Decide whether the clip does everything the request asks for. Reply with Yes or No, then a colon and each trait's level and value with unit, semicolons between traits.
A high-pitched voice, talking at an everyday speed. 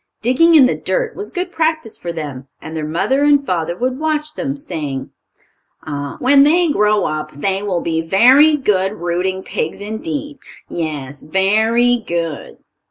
Yes: high, 210 Hz; average, 160 wpm